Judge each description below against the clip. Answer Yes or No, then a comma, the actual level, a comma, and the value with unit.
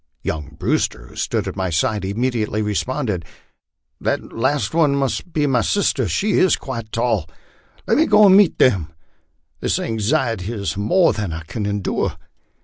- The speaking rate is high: No, average, 165 wpm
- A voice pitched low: Yes, low, 115 Hz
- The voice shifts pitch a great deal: Yes, wide, 5.9 semitones